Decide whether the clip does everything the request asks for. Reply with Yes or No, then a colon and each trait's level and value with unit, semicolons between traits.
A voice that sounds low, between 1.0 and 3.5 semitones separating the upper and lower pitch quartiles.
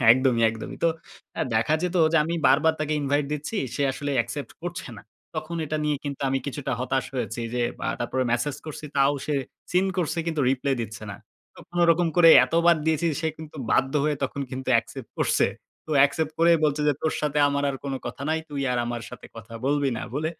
No: medium, 145 Hz; average, 3.2 semitones